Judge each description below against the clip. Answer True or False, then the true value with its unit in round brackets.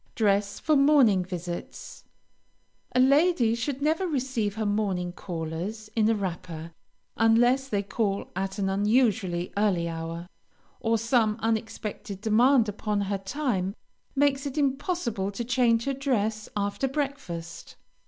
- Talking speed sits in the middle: False (130 wpm)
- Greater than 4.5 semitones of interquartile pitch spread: True (5.0 semitones)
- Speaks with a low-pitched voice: False (215 Hz)